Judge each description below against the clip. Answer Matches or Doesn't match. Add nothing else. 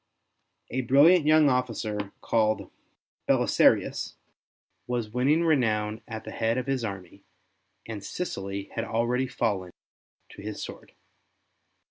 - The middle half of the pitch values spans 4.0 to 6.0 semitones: Doesn't match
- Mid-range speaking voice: Doesn't match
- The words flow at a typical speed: Doesn't match